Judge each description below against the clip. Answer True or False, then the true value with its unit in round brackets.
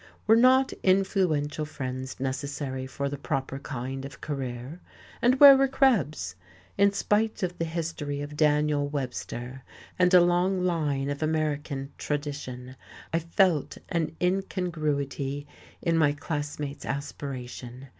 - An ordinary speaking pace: False (125 wpm)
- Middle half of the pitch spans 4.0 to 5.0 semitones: True (4.3 semitones)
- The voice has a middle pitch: True (150 Hz)